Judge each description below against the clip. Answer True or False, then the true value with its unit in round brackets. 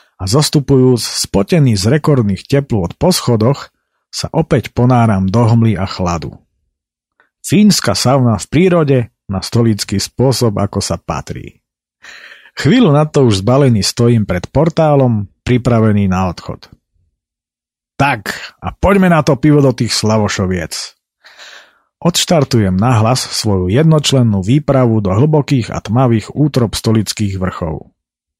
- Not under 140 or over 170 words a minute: False (120 wpm)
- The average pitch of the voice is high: False (120 Hz)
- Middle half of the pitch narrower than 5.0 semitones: False (6.0 semitones)